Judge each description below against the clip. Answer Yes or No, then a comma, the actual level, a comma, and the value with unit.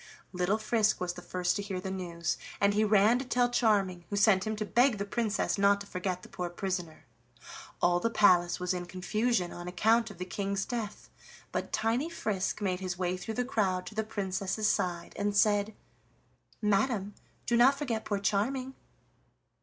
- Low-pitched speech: No, high, 200 Hz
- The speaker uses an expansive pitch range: No, average, 3.2 semitones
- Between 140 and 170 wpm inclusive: No, average, 185 wpm